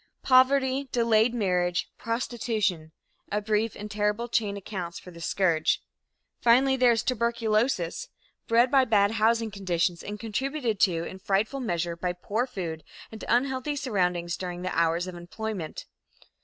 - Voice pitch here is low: No, high, 210 Hz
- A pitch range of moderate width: Yes, average, 4.9 semitones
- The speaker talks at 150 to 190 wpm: No, average, 140 wpm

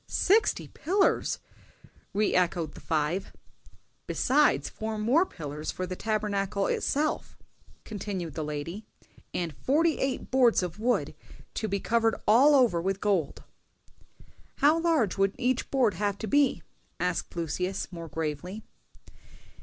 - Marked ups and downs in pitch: Yes, wide, 6.2 semitones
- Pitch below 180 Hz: No, high, 205 Hz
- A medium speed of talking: No, slow, 130 wpm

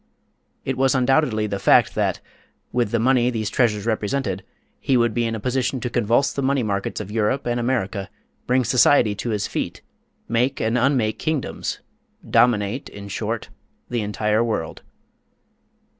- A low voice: Yes, low, 120 Hz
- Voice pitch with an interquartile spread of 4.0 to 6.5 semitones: No, average, 3.3 semitones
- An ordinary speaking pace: Yes, average, 160 wpm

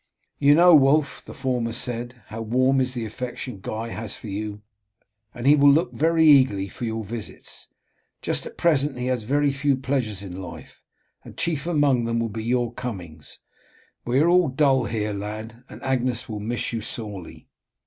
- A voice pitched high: No, low, 125 Hz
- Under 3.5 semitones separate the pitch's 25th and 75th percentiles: No, average, 4.1 semitones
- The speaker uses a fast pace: No, average, 180 wpm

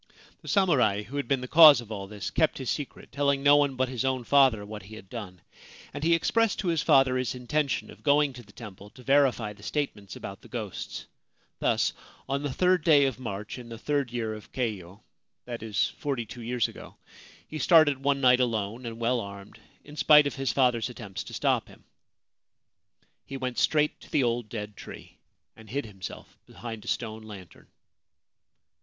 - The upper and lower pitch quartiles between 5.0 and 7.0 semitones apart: No, average, 4.6 semitones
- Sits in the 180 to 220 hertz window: No, low, 125 Hz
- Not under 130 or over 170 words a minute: No, average, 200 wpm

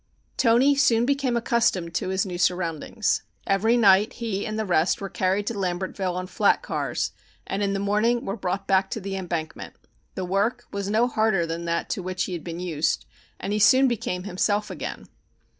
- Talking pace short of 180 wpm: No, average, 190 wpm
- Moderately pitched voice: No, high, 195 Hz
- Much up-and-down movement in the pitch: No, average, 3.5 semitones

